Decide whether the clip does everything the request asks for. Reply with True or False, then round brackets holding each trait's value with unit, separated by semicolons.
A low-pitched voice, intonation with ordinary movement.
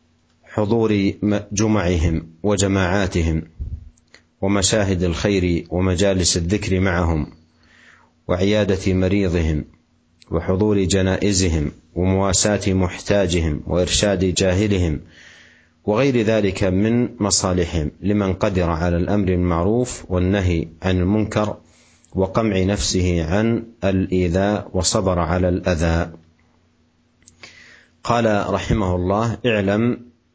True (95 Hz; 3.4 semitones)